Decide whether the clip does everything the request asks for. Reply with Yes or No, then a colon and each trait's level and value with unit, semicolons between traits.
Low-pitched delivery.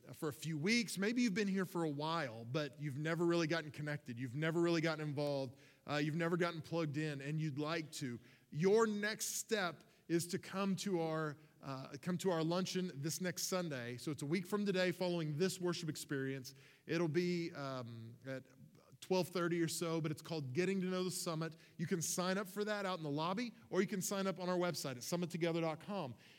No: medium, 165 Hz